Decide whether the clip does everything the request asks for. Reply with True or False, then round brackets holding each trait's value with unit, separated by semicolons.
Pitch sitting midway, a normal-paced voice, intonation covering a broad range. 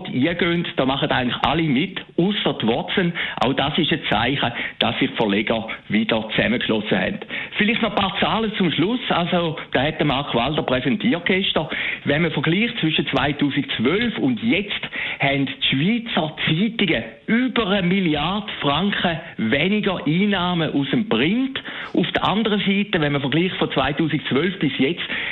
True (170 Hz; 150 wpm; 6.1 semitones)